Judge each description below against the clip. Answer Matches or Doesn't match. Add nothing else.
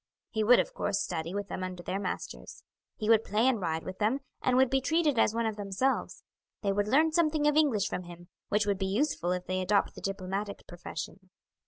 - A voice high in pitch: Matches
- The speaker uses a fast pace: Matches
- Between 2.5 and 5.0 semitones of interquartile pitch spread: Doesn't match